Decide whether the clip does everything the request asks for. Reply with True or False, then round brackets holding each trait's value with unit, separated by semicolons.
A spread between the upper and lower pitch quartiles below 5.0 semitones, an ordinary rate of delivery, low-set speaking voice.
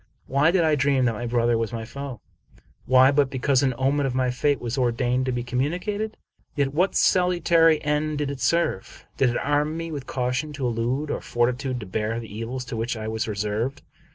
False (3.6 semitones; 210 wpm; 130 Hz)